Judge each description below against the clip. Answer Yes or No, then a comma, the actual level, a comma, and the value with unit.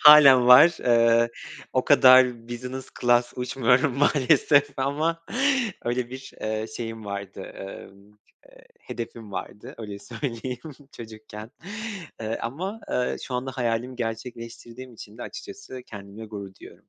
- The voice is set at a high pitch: No, low, 120 Hz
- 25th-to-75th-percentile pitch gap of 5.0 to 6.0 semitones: No, average, 2.7 semitones